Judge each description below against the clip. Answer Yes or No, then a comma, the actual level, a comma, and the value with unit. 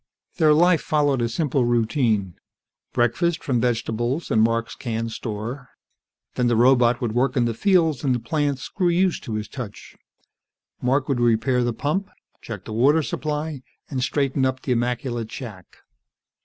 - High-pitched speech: No, low, 125 Hz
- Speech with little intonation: No, average, 3.9 semitones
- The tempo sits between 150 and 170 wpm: Yes, average, 160 wpm